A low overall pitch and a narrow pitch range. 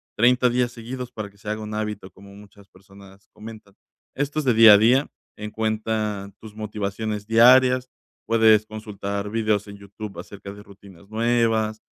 Yes: low, 110 Hz; narrow, 2.0 semitones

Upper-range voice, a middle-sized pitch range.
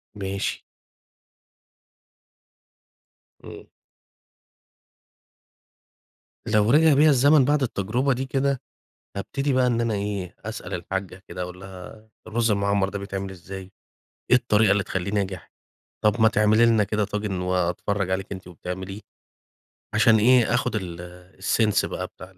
No: low, 105 Hz; average, 3.6 semitones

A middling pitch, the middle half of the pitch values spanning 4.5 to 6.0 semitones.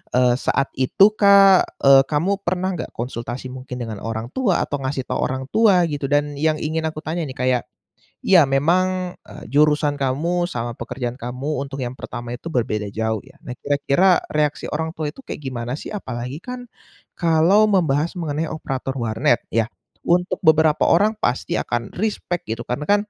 Yes: medium, 145 Hz; wide, 5.4 semitones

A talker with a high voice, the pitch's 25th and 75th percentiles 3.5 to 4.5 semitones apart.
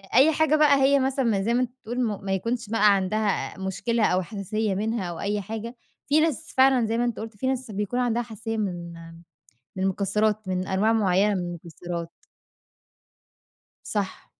Yes: high, 215 Hz; average, 3.9 semitones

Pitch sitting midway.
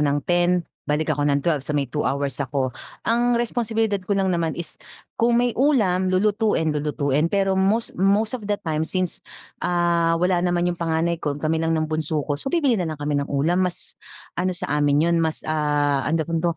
Yes: medium, 170 Hz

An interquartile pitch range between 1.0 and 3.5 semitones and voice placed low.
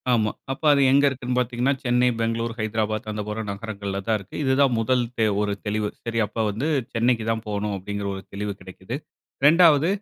Yes: average, 3.2 semitones; low, 115 Hz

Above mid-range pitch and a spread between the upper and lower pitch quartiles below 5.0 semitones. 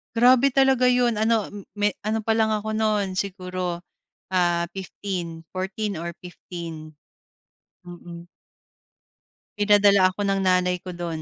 Yes: high, 195 Hz; average, 3.6 semitones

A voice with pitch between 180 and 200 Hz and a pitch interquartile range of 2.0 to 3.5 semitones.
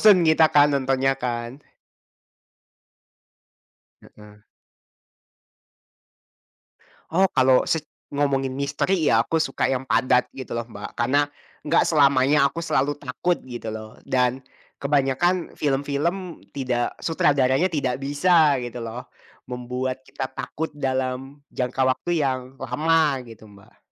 No: low, 135 Hz; average, 2.8 semitones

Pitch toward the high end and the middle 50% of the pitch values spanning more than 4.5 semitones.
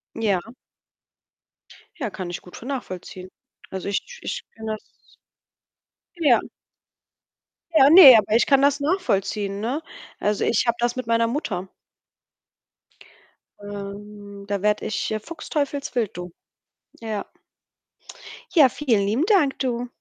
Yes: high, 225 Hz; average, 5.2 semitones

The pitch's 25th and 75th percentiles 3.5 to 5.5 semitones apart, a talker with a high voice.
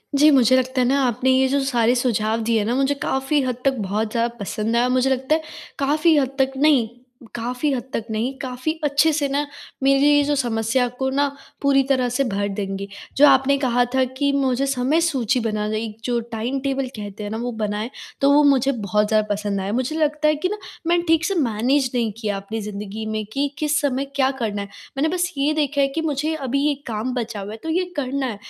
Yes: average, 4.0 semitones; very high, 260 Hz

